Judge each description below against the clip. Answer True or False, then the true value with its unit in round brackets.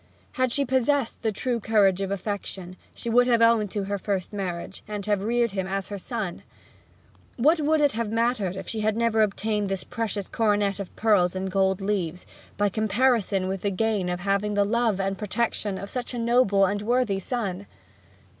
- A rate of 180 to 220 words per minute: True (190 wpm)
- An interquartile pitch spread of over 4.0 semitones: False (3.1 semitones)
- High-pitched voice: True (205 Hz)